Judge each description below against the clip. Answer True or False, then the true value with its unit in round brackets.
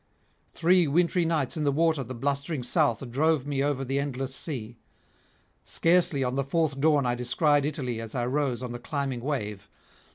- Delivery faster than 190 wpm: False (175 wpm)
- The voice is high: False (140 Hz)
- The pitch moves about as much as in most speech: True (3.5 semitones)